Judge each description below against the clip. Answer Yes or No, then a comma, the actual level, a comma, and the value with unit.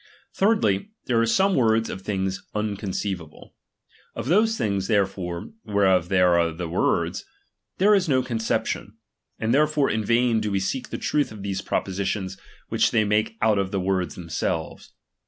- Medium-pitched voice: No, low, 105 Hz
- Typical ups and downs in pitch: Yes, average, 3.8 semitones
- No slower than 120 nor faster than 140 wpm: No, average, 165 wpm